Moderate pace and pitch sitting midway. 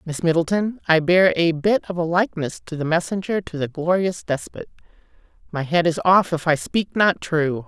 Yes: average, 190 wpm; medium, 170 Hz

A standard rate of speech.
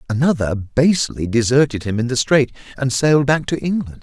Yes: average, 180 wpm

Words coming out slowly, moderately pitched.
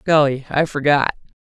Yes: slow, 125 wpm; medium, 145 Hz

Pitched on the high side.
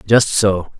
No: low, 100 Hz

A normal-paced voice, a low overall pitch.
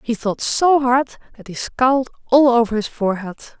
No: average, 185 wpm; high, 240 Hz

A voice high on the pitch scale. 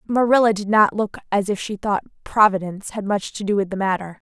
Yes: high, 205 Hz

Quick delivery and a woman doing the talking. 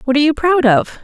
Yes: fast, 290 wpm; female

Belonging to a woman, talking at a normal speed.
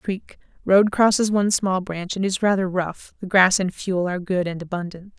Yes: female; average, 195 wpm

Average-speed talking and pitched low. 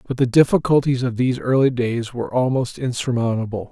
Yes: average, 160 wpm; low, 125 Hz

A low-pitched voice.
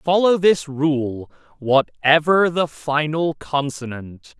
No: medium, 150 Hz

